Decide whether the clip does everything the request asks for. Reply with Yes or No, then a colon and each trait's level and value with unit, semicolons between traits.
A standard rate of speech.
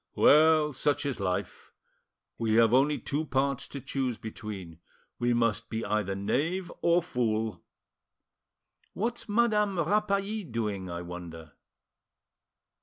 No: slow, 115 wpm